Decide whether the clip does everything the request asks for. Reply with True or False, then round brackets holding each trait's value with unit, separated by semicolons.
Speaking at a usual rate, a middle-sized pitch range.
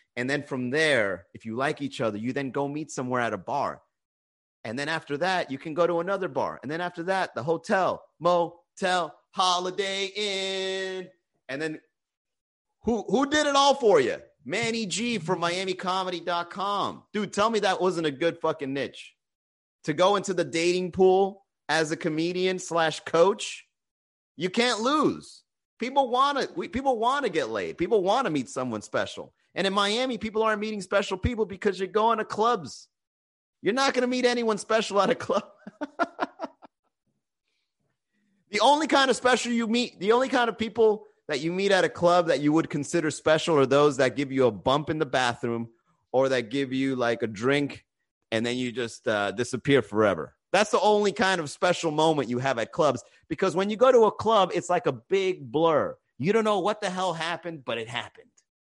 False (190 wpm; 7.2 semitones)